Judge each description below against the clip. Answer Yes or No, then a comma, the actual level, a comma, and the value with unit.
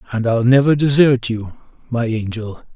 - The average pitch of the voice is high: No, low, 120 Hz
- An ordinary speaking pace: Yes, average, 155 wpm